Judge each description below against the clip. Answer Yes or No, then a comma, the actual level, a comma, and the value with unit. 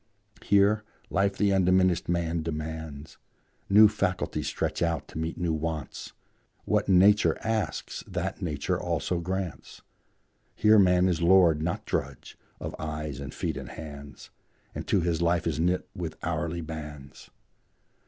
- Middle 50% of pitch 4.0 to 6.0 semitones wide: No, average, 3.0 semitones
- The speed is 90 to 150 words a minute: Yes, average, 140 wpm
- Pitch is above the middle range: No, very low, 85 Hz